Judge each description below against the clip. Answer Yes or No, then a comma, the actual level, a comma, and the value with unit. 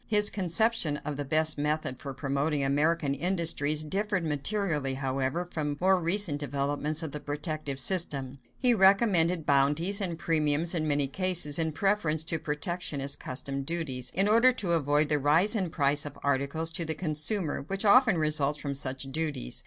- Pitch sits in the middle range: Yes, medium, 155 Hz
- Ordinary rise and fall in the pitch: Yes, average, 3.7 semitones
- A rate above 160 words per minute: Yes, average, 170 wpm